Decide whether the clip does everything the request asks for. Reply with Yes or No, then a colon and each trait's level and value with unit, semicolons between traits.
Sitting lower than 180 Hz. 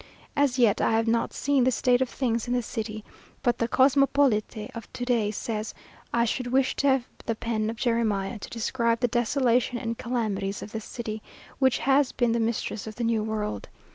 No: high, 235 Hz